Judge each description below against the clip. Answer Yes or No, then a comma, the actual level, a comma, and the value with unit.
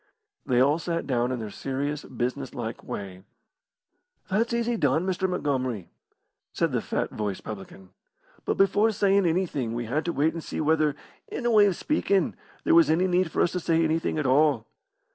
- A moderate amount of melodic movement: No, wide, 6.2 semitones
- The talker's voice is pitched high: No, medium, 155 Hz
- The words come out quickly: No, average, 185 wpm